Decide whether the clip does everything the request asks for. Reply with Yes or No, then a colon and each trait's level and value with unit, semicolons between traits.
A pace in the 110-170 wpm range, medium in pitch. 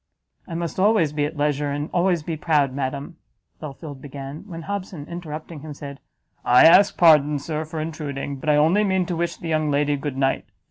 No: average, 195 wpm; medium, 155 Hz